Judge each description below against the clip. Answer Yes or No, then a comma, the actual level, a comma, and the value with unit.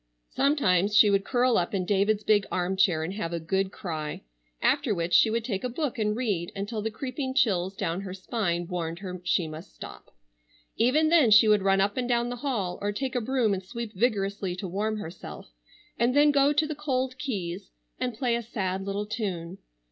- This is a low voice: No, high, 205 Hz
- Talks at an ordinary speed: No, fast, 210 wpm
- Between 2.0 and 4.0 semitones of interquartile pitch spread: No, average, 4.7 semitones